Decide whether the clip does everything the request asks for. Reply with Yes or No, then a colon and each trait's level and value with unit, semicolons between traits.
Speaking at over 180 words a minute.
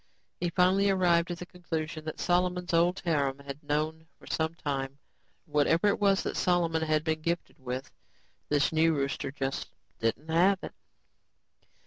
No: average, 155 wpm